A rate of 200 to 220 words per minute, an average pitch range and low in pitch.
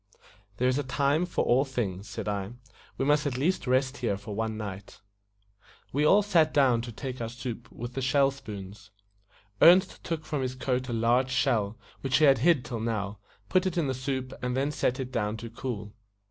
Yes: fast, 205 wpm; average, 3.7 semitones; low, 130 Hz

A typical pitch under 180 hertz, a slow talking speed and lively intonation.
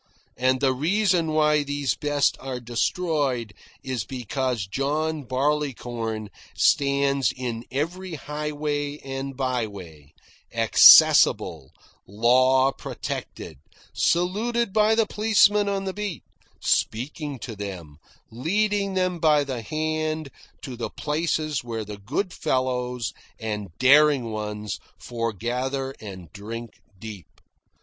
No: low, 135 Hz; slow, 110 wpm; average, 5.0 semitones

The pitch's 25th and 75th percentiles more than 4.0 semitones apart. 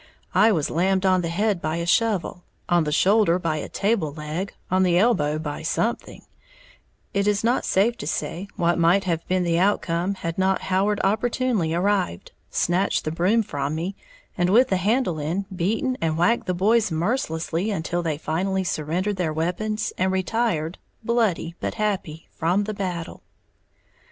No: average, 3.7 semitones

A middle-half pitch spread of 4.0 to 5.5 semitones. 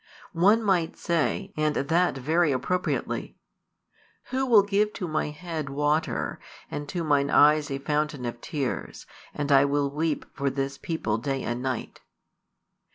No: average, 3.5 semitones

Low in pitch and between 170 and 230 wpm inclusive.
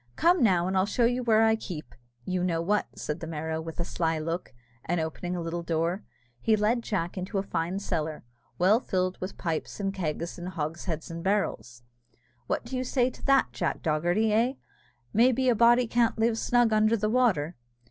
No: medium, 185 Hz; average, 200 wpm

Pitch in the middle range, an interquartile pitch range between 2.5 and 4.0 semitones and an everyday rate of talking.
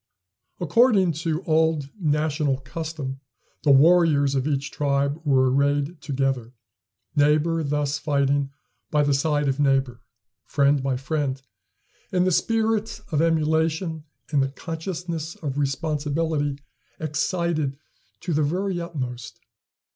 No: medium, 150 Hz; average, 2.8 semitones; slow, 115 wpm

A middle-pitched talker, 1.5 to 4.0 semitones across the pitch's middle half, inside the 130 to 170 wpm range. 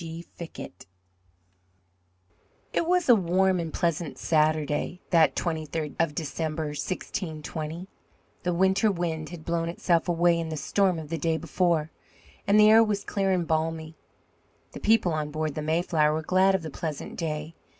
Yes: medium, 165 Hz; narrow, 2.6 semitones; average, 160 wpm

